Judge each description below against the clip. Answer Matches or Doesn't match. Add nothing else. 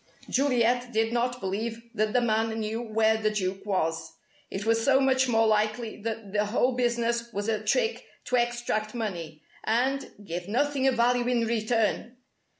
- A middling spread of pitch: Doesn't match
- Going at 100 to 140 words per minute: Doesn't match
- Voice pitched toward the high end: Matches